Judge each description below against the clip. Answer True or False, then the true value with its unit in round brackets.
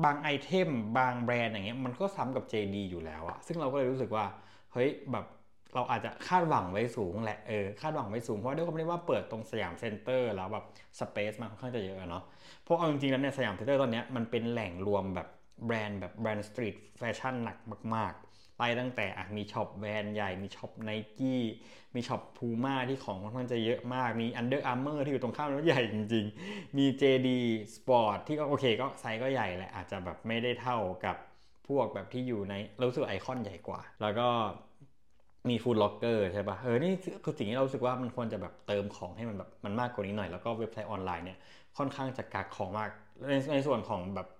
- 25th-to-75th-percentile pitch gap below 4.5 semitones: True (3.7 semitones)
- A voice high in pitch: False (115 Hz)